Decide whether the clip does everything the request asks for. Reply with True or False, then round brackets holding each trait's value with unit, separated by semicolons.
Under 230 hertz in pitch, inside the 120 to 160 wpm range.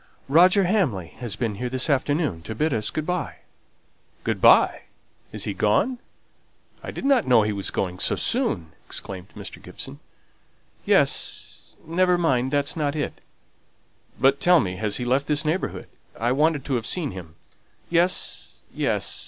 True (140 Hz; 155 wpm)